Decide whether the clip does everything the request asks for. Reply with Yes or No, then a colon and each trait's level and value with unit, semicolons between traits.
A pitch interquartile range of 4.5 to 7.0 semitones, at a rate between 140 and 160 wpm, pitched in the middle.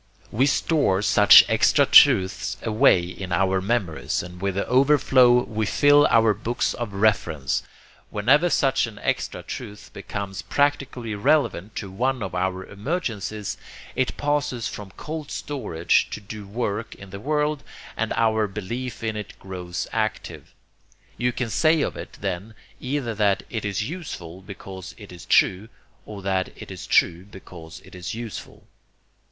No: average, 4.9 semitones; average, 150 wpm; low, 105 Hz